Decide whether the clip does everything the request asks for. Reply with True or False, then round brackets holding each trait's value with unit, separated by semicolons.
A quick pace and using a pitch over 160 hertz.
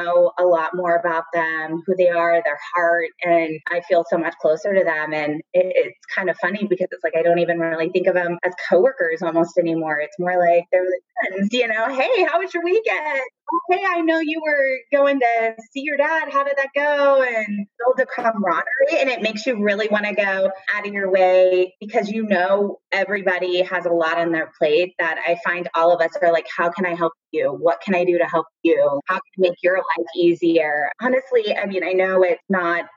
True (225 wpm; 185 Hz)